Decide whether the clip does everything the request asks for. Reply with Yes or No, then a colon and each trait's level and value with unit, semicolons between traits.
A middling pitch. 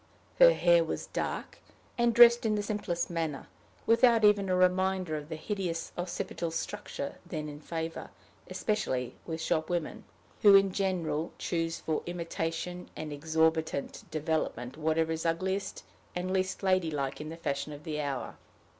Yes: medium, 165 Hz